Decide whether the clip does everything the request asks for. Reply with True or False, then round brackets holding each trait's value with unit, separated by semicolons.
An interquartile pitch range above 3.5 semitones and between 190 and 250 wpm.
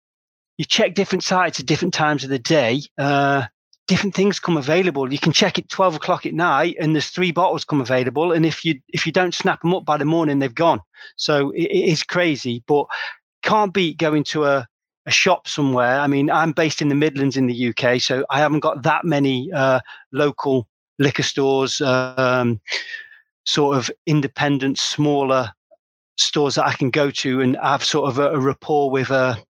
True (4.0 semitones; 200 wpm)